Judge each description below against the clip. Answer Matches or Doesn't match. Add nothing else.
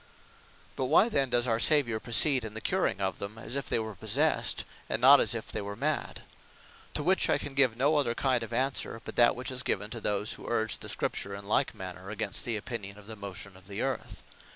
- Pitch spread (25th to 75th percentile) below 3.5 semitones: Doesn't match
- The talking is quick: Matches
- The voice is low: Matches